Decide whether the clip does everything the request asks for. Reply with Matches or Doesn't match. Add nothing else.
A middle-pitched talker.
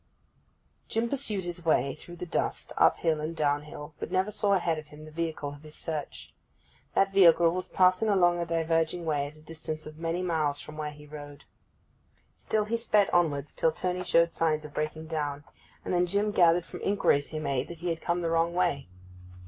Matches